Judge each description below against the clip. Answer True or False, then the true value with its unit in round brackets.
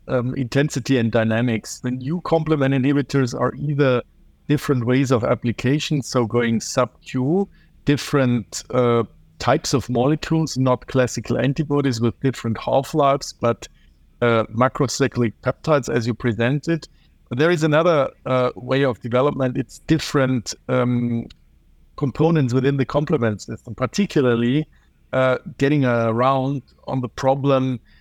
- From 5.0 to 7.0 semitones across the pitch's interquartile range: False (3.0 semitones)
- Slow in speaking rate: True (130 wpm)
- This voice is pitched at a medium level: False (130 Hz)